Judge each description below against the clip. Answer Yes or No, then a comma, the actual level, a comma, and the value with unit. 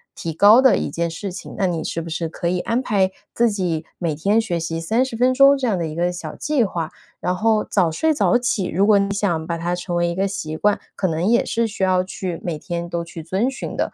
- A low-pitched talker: No, medium, 185 Hz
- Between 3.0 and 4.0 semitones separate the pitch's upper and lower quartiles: No, average, 4.5 semitones